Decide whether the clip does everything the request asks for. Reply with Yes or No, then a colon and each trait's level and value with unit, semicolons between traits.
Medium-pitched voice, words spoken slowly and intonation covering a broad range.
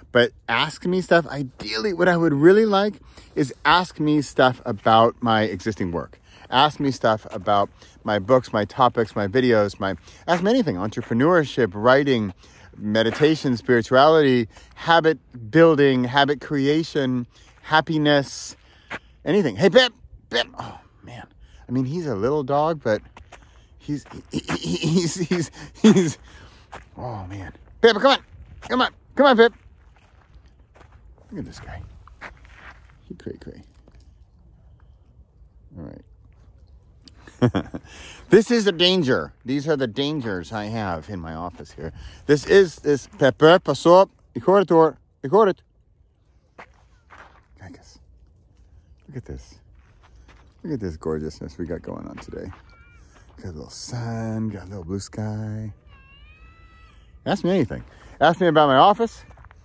No: low, 115 Hz; slow, 130 wpm; wide, 8.7 semitones